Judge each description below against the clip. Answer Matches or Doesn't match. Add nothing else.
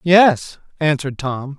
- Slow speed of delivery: Matches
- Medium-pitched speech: Matches